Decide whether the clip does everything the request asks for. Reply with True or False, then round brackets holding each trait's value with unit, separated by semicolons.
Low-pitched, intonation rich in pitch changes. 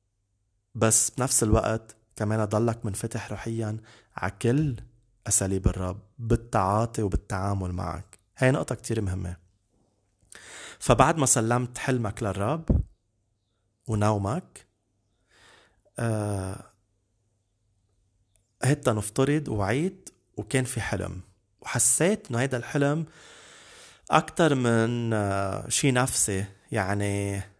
False (110 Hz; 3.2 semitones)